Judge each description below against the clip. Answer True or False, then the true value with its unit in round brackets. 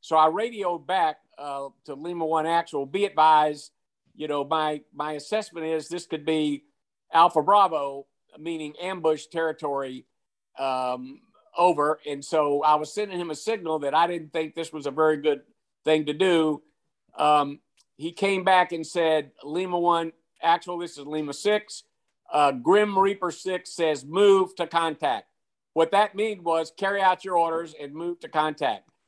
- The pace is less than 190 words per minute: True (165 wpm)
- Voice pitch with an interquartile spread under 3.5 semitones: True (2.9 semitones)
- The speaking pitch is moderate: True (160 Hz)